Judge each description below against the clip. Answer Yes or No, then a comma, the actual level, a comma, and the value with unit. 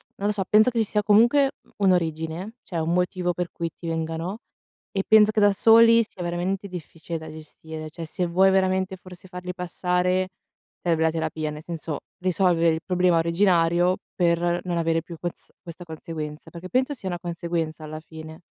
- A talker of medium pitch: Yes, medium, 175 Hz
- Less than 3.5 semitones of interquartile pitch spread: Yes, narrow, 2.6 semitones